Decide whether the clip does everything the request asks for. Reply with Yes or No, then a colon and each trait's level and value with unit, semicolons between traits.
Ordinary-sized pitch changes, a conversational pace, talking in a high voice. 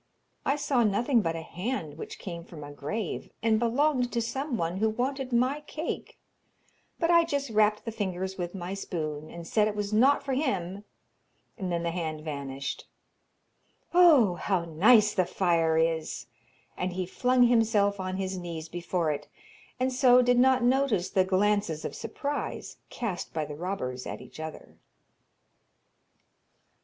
No: wide, 6.4 semitones; average, 160 wpm; high, 200 Hz